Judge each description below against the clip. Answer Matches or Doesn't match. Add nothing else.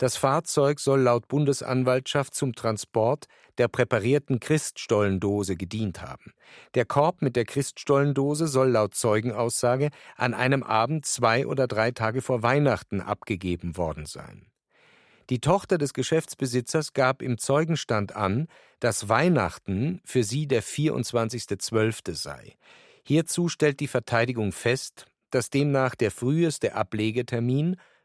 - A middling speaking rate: Doesn't match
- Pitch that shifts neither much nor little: Matches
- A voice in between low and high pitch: Doesn't match